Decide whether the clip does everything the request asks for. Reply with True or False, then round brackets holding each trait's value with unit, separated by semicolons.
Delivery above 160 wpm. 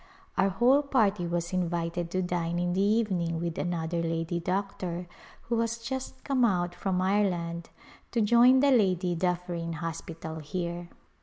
False (155 wpm)